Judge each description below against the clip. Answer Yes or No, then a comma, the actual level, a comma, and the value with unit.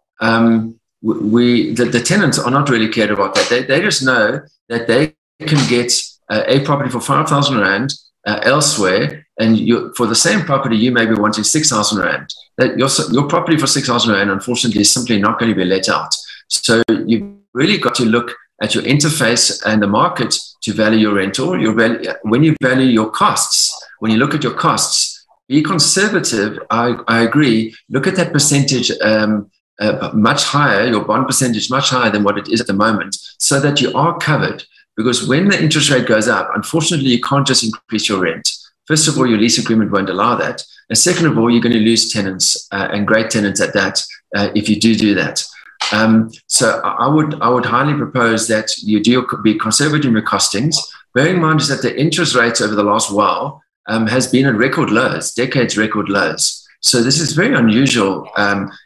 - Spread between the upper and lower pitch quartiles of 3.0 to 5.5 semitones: Yes, average, 4.3 semitones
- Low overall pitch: Yes, low, 115 Hz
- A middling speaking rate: No, fast, 210 wpm